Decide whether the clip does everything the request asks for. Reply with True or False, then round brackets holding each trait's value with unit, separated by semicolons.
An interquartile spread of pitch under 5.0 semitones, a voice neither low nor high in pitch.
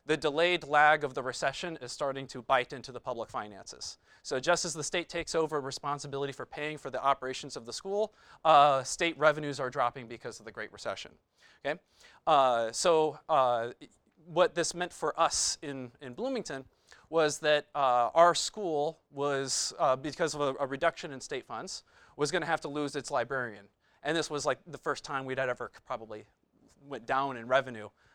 True (3.5 semitones; 145 Hz)